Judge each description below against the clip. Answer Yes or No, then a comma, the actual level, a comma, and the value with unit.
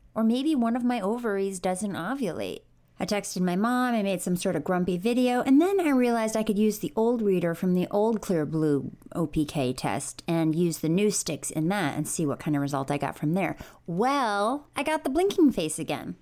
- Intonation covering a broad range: Yes, wide, 6.4 semitones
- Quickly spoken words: Yes, fast, 220 wpm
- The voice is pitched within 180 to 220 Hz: Yes, high, 190 Hz